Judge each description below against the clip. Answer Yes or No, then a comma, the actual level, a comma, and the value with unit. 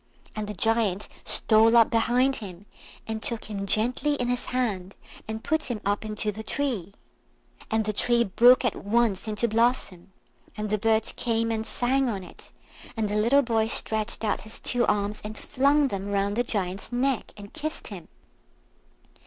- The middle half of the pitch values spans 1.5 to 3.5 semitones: Yes, average, 2.9 semitones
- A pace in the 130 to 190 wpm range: Yes, average, 175 wpm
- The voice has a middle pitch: No, high, 220 Hz